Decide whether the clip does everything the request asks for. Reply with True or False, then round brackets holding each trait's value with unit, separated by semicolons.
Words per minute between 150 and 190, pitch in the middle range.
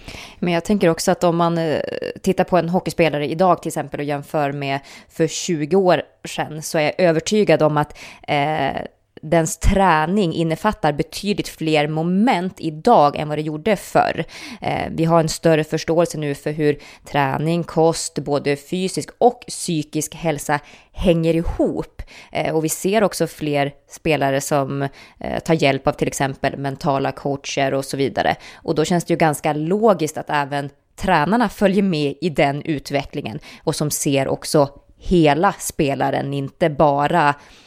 True (160 wpm; 160 Hz)